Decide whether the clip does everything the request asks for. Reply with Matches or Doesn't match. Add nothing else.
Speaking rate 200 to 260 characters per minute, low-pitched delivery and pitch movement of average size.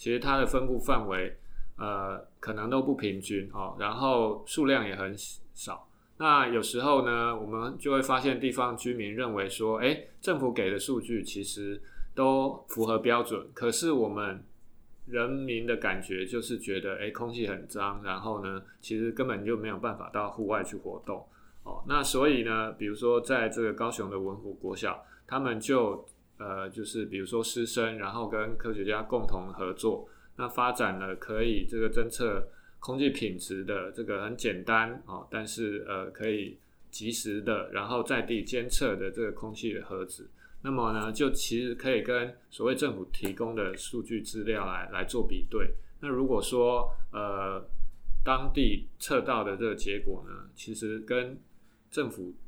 Matches